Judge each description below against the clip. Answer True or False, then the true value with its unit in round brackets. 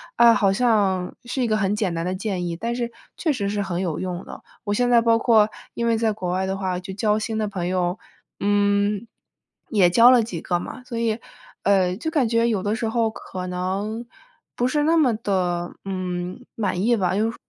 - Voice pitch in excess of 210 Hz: False (205 Hz)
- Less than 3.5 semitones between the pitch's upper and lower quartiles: False (3.8 semitones)